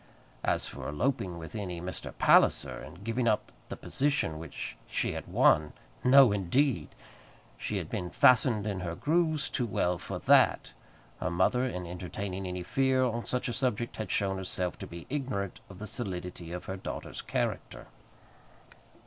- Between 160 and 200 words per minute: Yes, average, 165 wpm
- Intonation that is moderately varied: No, wide, 5.8 semitones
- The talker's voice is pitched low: Yes, low, 100 Hz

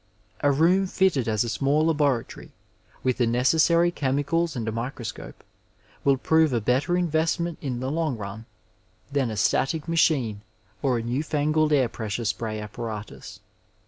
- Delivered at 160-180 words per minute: No, average, 150 wpm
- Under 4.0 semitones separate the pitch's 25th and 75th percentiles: No, average, 5.3 semitones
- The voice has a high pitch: No, low, 135 Hz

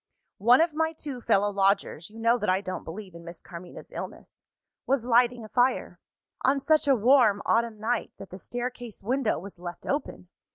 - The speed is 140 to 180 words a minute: No, average, 190 wpm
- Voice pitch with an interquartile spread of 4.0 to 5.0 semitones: Yes, average, 4.4 semitones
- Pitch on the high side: Yes, high, 230 Hz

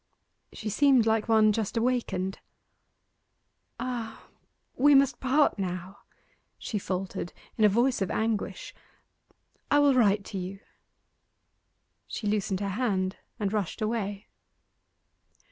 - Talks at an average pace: No, slow, 115 wpm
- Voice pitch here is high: Yes, high, 215 Hz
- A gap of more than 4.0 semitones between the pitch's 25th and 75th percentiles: No, average, 3.7 semitones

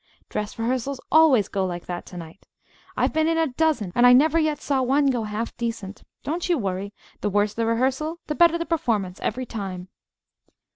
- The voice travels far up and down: Yes, wide, 6.8 semitones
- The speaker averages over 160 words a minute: Yes, average, 195 wpm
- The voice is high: Yes, high, 245 Hz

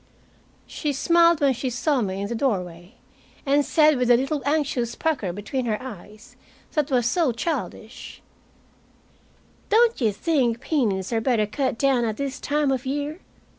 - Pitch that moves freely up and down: No, average, 4.6 semitones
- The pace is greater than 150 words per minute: Yes, average, 160 wpm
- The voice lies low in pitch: No, very high, 260 Hz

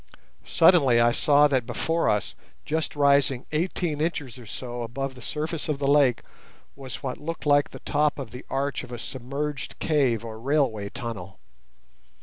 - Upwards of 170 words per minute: No, average, 165 wpm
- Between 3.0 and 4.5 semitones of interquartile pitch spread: Yes, average, 3.5 semitones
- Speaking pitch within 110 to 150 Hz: Yes, medium, 140 Hz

